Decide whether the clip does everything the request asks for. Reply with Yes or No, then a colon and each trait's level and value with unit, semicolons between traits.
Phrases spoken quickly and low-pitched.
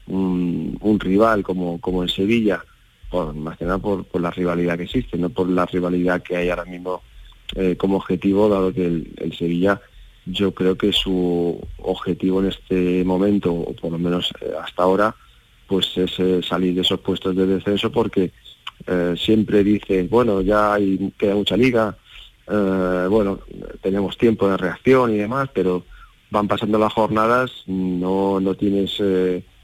No: average, 170 wpm; very low, 95 Hz